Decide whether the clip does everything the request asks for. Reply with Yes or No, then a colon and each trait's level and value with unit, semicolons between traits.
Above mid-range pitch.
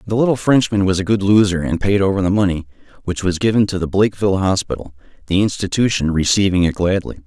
No: very low, 95 Hz